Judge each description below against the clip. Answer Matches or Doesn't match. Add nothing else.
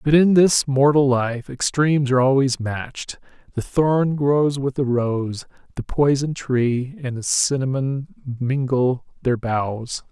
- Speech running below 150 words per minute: Matches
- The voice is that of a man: Matches